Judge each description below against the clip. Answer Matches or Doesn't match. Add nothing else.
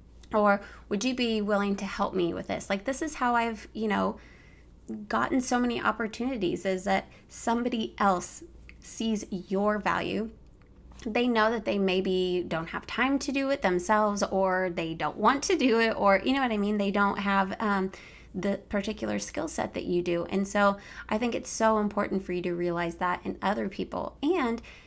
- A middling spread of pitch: Matches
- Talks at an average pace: Matches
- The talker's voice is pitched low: Doesn't match